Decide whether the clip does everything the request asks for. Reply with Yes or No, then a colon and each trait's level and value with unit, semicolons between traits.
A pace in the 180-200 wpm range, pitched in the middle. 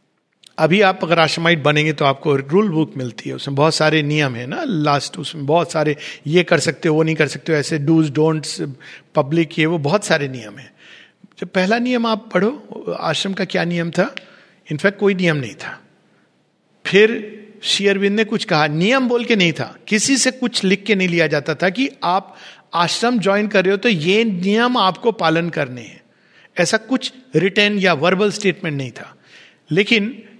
Yes: fast, 190 wpm; medium, 175 Hz